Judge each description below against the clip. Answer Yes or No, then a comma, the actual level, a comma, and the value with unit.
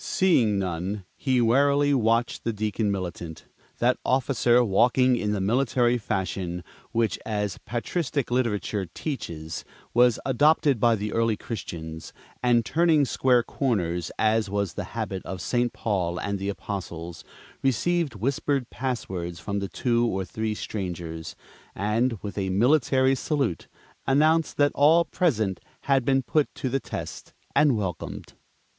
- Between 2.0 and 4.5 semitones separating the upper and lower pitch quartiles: No, average, 5.3 semitones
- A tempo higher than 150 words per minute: No, average, 140 wpm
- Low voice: Yes, low, 115 Hz